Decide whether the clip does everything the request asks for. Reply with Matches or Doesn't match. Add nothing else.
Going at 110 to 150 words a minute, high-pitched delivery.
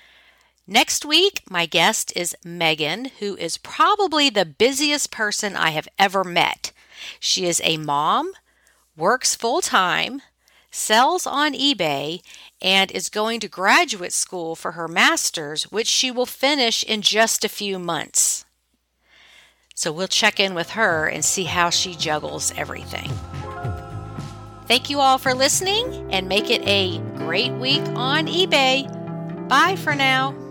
Matches